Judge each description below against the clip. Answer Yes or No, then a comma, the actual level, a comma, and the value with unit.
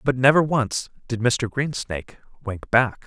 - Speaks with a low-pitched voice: Yes, low, 120 Hz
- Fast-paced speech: No, average, 155 wpm